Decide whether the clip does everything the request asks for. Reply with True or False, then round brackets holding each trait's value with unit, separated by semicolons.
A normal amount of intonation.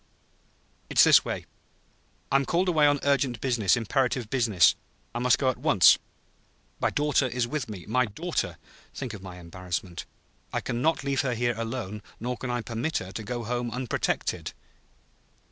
True (3.9 semitones)